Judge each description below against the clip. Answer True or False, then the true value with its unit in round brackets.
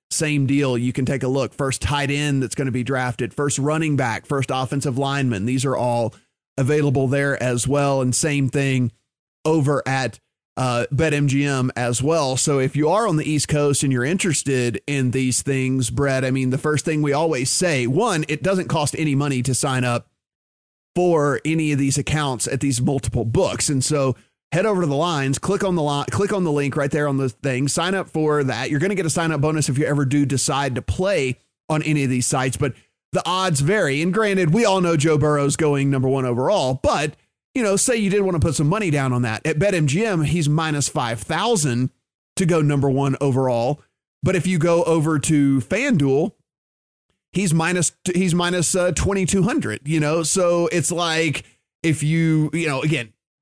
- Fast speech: True (210 wpm)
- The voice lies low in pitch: False (145 Hz)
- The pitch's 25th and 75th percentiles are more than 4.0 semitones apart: False (3.5 semitones)